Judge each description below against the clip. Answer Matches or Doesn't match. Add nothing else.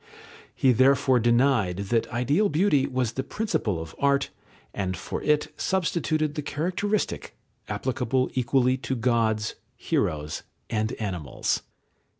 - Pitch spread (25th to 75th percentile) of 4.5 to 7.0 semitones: Matches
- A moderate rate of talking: Doesn't match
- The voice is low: Matches